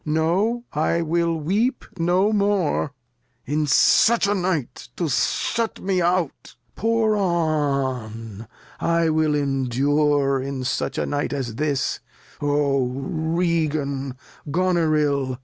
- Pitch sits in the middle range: Yes, medium, 155 Hz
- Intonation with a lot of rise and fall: No, average, 4.2 semitones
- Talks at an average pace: No, slow, 105 wpm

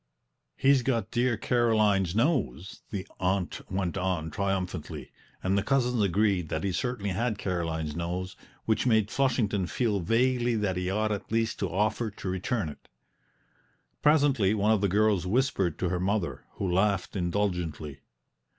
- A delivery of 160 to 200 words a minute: No, average, 150 wpm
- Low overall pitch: Yes, low, 100 Hz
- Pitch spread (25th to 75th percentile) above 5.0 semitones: No, average, 3.8 semitones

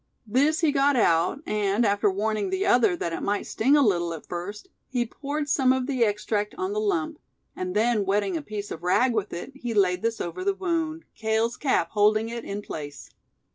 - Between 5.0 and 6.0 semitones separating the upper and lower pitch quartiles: Yes, wide, 5.6 semitones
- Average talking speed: No, fast, 210 wpm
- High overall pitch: Yes, high, 220 Hz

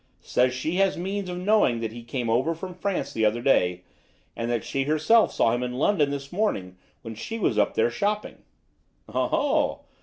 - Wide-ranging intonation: Yes, wide, 8.4 semitones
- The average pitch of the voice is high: No, medium, 140 Hz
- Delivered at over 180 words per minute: Yes, average, 190 wpm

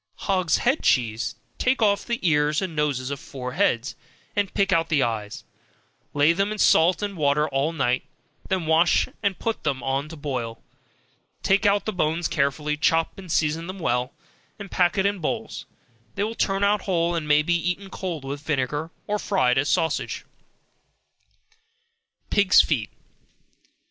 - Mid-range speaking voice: Yes, medium, 160 Hz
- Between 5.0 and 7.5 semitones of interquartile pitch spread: Yes, wide, 5.5 semitones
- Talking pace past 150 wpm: Yes, average, 170 wpm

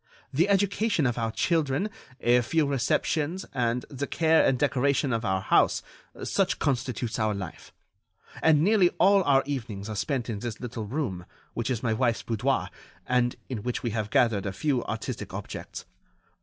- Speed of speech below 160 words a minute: No, average, 165 wpm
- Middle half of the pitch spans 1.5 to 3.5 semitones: No, average, 4.5 semitones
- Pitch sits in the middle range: No, low, 125 Hz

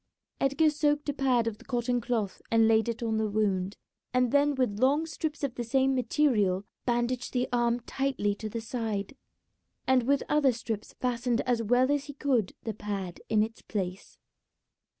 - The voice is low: No, high, 240 Hz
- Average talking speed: Yes, average, 180 wpm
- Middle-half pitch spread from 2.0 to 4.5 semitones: Yes, average, 3.6 semitones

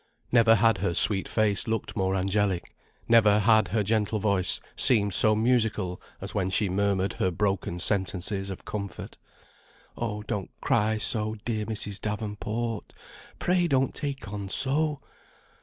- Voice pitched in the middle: No, low, 105 Hz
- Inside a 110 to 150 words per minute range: Yes, average, 140 wpm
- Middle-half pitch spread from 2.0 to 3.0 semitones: Yes, narrow, 2.4 semitones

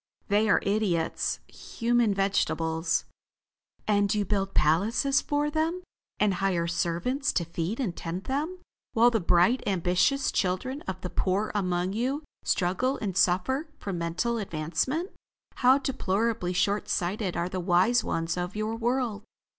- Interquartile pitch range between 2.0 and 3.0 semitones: No, average, 5.3 semitones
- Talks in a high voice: Yes, high, 200 Hz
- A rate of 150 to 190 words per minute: No, average, 140 wpm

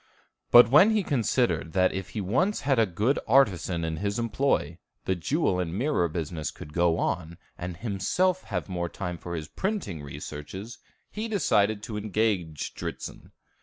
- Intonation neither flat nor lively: No, wide, 6.2 semitones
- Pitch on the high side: No, low, 100 Hz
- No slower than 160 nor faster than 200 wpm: Yes, average, 165 wpm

